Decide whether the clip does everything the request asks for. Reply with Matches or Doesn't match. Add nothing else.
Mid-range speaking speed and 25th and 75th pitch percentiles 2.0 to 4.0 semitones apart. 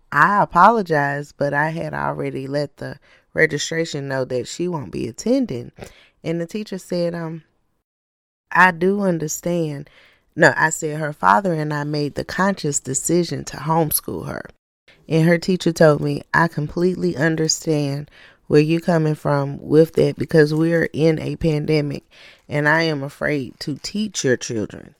Matches